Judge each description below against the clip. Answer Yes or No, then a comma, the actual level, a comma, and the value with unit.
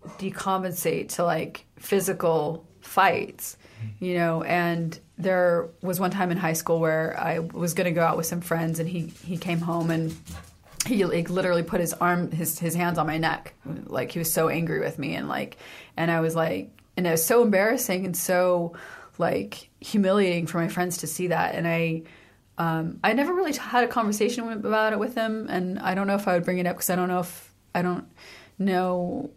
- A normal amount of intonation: No, narrow, 2.2 semitones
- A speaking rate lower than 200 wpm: No, fast, 205 wpm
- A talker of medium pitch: Yes, medium, 175 Hz